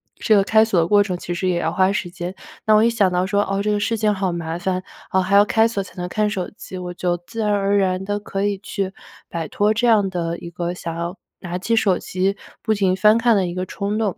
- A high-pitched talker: Yes, high, 195 Hz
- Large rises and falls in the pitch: No, average, 2.7 semitones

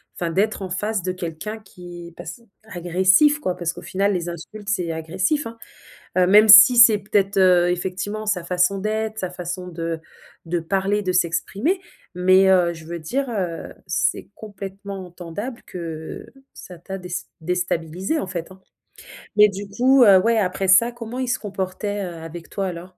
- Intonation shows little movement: No, average, 3.1 semitones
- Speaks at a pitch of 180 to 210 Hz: Yes, high, 190 Hz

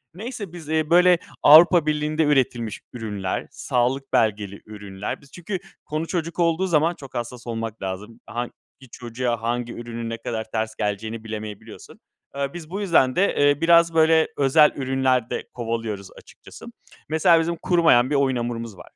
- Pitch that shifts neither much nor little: No, wide, 6.0 semitones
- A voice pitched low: Yes, low, 130 Hz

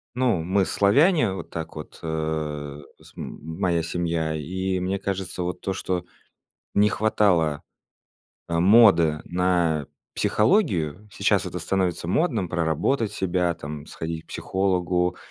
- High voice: No, very low, 90 Hz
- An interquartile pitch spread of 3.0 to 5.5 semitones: Yes, average, 3.3 semitones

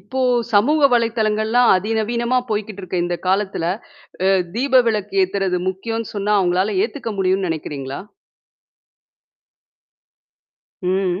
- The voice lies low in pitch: No, high, 210 Hz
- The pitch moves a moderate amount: Yes, average, 3.4 semitones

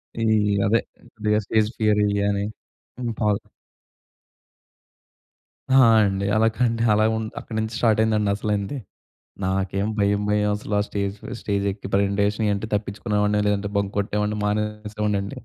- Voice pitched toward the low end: Yes, low, 105 Hz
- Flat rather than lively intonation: Yes, narrow, 1.1 semitones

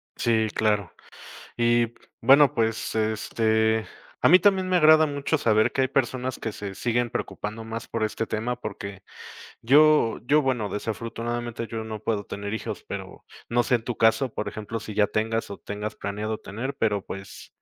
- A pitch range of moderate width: No, narrow, 2.3 semitones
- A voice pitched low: Yes, low, 115 Hz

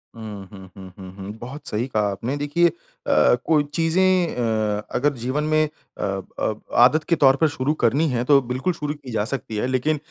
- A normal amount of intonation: No, wide, 5.8 semitones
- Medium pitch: No, low, 130 Hz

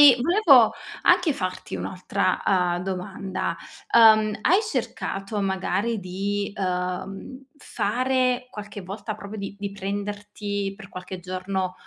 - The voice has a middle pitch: No, high, 200 Hz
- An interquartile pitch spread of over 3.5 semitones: No, average, 3.0 semitones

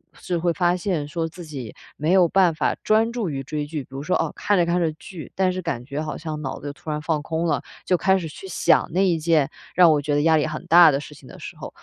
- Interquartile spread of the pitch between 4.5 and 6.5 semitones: No, average, 3.0 semitones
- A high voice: No, medium, 160 Hz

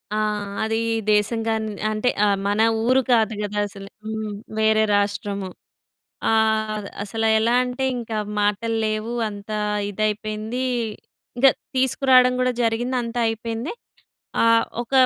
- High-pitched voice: Yes, high, 220 Hz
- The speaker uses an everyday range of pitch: No, narrow, 2.0 semitones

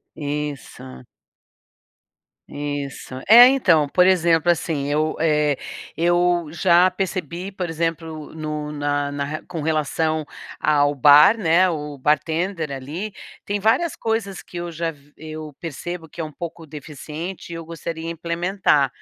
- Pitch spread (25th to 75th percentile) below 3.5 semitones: Yes, average, 2.8 semitones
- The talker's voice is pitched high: No, medium, 160 Hz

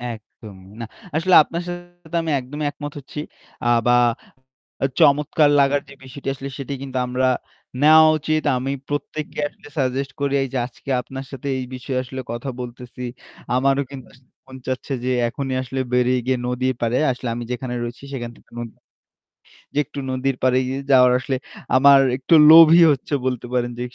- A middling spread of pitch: No, narrow, 2.3 semitones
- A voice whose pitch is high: No, low, 130 Hz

